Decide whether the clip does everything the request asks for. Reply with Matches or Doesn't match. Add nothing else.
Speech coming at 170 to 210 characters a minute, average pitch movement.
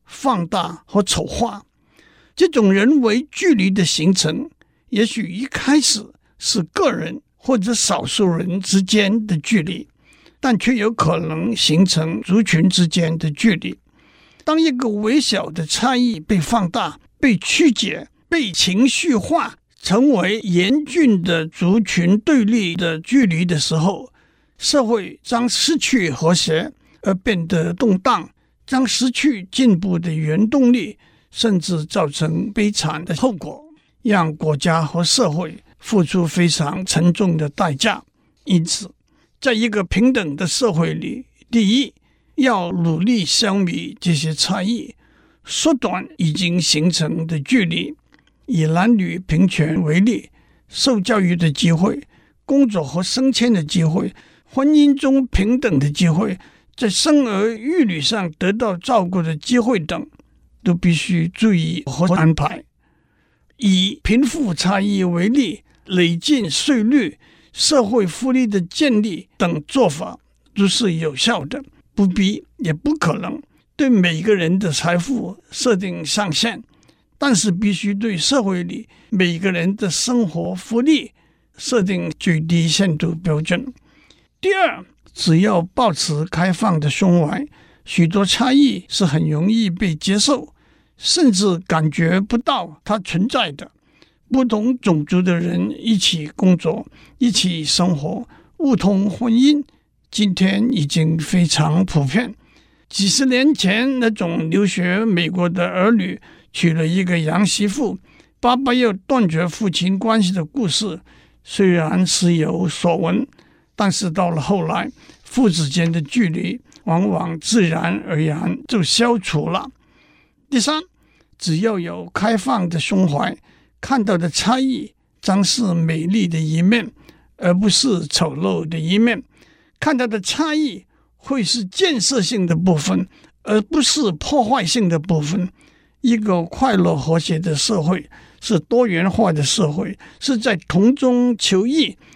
Doesn't match